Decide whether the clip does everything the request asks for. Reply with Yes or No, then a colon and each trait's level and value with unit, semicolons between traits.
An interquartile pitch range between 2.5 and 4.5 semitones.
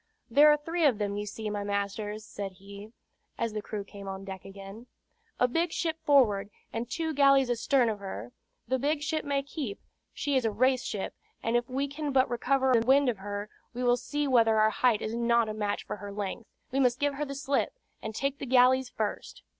No: average, 4.9 semitones